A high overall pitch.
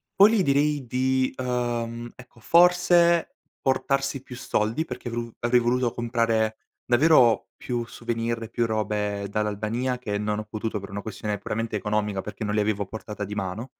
No: low, 115 Hz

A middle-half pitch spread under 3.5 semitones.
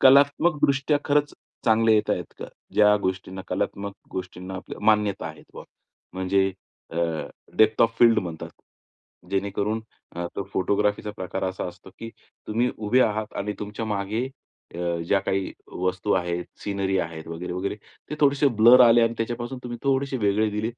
No: average, 3.8 semitones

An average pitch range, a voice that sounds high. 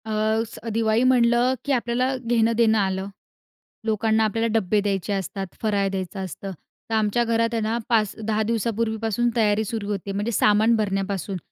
No: narrow, 2.3 semitones; high, 220 Hz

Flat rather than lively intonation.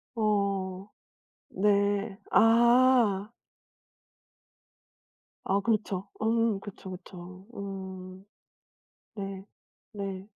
Yes: narrow, 2.1 semitones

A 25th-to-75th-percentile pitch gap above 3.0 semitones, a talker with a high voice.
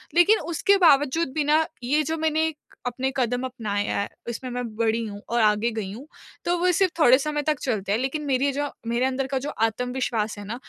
Yes: average, 4.7 semitones; very high, 260 Hz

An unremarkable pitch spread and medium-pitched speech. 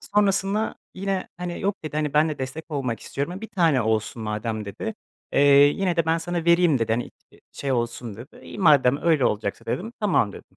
No: wide, 7.0 semitones; medium, 155 Hz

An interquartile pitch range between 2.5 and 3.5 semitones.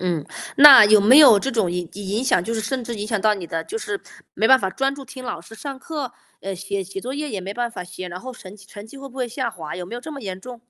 No: wide, 5.5 semitones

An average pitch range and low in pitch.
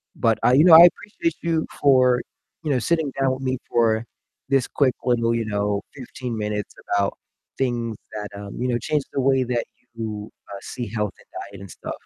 Yes: average, 3.8 semitones; low, 120 Hz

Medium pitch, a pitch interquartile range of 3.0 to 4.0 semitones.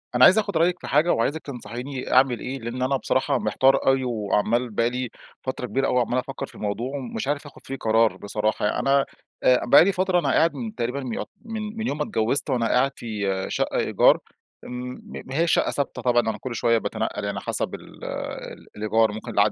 No: low, 125 Hz; average, 3.7 semitones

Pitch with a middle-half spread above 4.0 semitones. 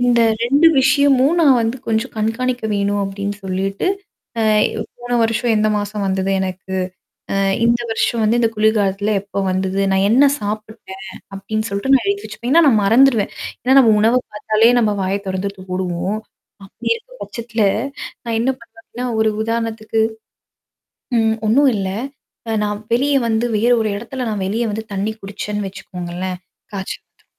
No: average, 3.2 semitones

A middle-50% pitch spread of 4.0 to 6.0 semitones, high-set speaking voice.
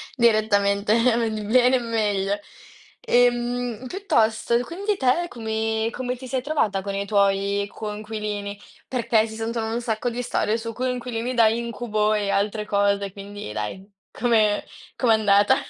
No: average, 2.9 semitones; high, 220 Hz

